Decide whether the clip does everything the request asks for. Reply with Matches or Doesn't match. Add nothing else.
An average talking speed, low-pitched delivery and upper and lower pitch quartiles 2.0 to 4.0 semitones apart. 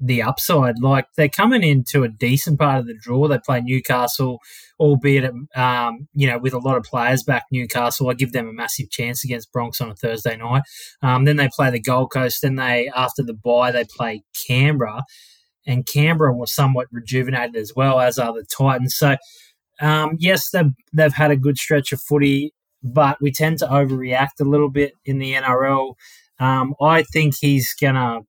Matches